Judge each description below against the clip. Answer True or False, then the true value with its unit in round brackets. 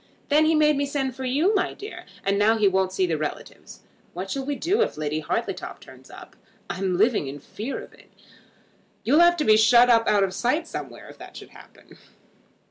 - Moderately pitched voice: False (235 Hz)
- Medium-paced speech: False (210 wpm)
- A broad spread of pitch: True (7.6 semitones)